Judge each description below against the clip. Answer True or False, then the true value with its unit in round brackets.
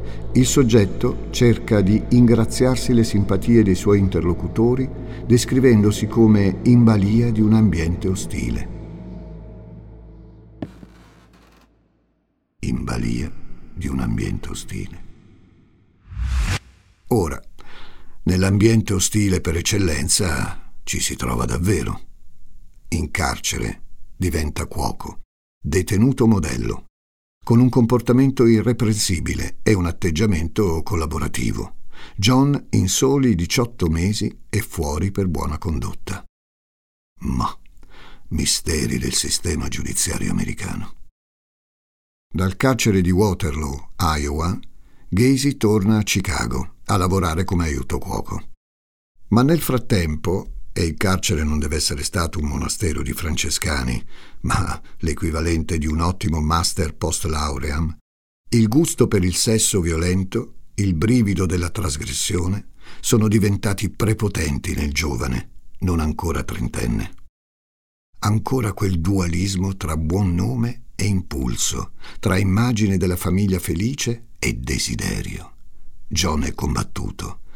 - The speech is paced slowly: True (105 wpm)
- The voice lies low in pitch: True (95 Hz)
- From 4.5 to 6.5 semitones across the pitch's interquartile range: True (5.0 semitones)